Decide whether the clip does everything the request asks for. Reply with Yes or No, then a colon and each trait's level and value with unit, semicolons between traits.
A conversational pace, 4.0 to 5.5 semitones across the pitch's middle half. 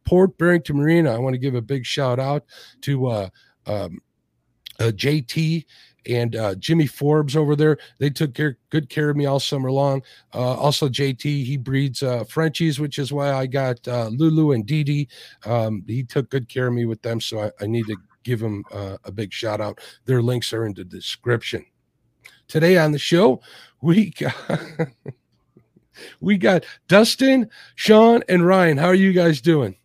Yes: average, 185 wpm; average, 4.6 semitones